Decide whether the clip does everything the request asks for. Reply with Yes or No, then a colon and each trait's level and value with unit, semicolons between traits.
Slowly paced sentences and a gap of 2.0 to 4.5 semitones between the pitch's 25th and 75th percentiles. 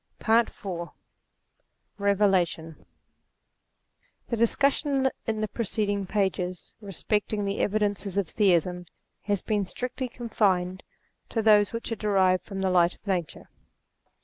Yes: slow, 120 wpm; average, 2.9 semitones